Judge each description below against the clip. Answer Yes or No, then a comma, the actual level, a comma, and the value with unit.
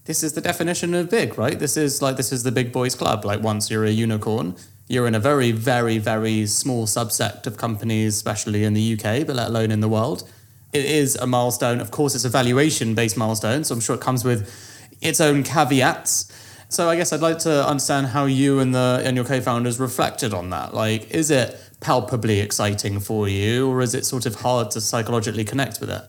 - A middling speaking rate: No, fast, 220 wpm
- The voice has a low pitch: Yes, low, 120 Hz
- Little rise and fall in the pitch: No, average, 3.9 semitones